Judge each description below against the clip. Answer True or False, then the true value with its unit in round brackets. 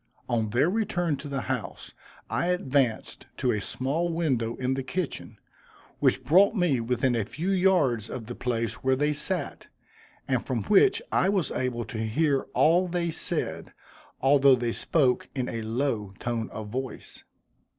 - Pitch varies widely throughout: True (6.1 semitones)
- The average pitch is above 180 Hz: False (135 Hz)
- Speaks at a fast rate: False (160 wpm)